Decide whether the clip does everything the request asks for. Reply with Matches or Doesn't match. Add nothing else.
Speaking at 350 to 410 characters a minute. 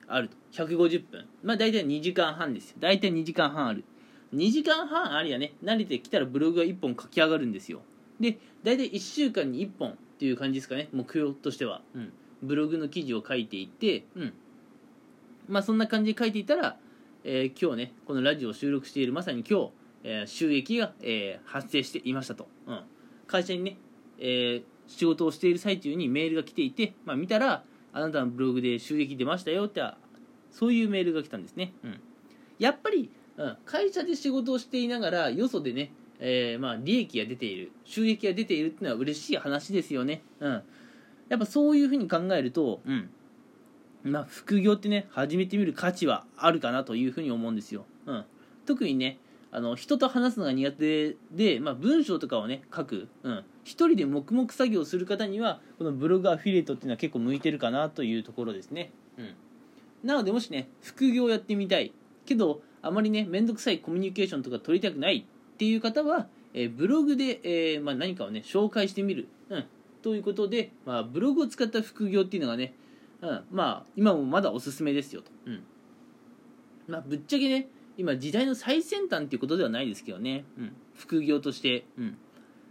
Matches